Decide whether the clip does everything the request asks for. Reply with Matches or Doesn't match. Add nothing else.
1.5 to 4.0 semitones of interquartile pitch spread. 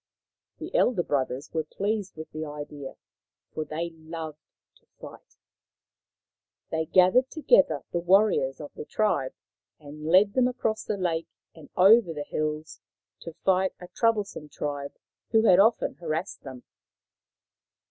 Doesn't match